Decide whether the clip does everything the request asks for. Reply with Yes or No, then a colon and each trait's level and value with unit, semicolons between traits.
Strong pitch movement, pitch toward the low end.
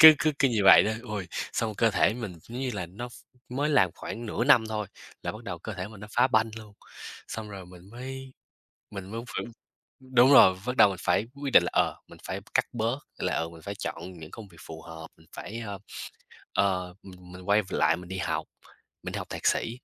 No: average, 4.6 semitones; low, 105 Hz